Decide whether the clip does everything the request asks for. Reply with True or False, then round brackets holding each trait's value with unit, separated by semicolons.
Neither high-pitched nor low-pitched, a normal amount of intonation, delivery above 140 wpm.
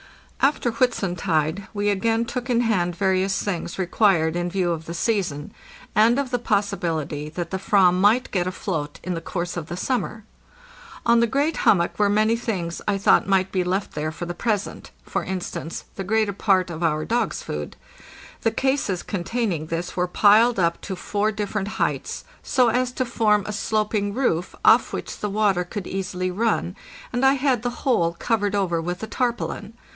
False (200 Hz; 4.4 semitones; 180 wpm)